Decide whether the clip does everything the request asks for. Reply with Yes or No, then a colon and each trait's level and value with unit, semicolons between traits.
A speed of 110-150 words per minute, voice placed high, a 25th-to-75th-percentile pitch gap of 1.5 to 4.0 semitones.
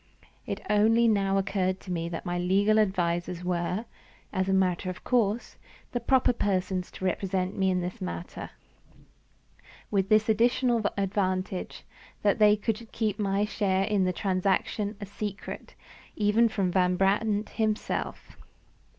Yes: average, 140 wpm; high, 195 Hz; narrow, 2.5 semitones